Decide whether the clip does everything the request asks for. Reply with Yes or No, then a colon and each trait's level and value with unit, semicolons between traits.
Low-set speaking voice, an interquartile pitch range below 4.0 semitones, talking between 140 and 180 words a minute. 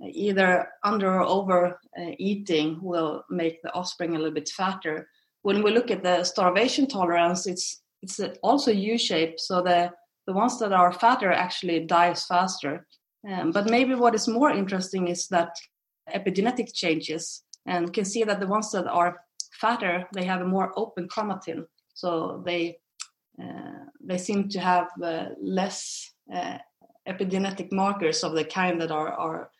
No: medium, 180 Hz; narrow, 2.6 semitones; average, 160 wpm